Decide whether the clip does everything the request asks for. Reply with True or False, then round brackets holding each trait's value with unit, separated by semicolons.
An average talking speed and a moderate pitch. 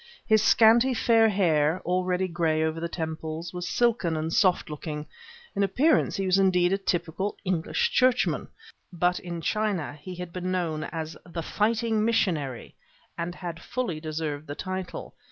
True (155 wpm; 180 Hz)